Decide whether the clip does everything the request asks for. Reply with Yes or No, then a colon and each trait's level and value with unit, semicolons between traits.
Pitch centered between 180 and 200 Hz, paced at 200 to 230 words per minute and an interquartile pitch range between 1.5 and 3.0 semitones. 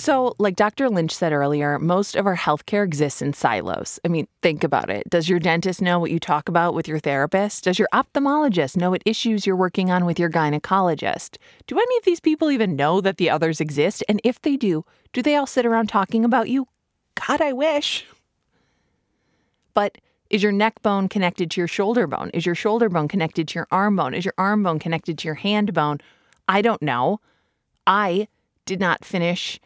No: high, 190 Hz; fast, 205 wpm; average, 4.9 semitones